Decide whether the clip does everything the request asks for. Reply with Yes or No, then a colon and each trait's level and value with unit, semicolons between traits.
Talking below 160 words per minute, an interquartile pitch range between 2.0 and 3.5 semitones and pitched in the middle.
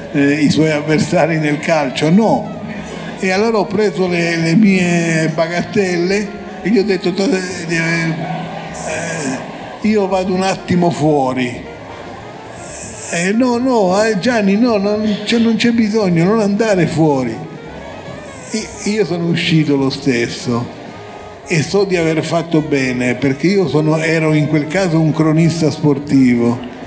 No: average, 140 wpm; average, 4.9 semitones; medium, 175 Hz